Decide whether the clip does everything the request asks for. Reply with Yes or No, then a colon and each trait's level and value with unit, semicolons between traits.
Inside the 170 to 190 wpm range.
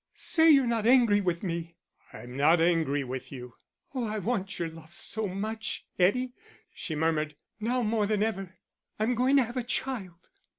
Yes: average, 175 wpm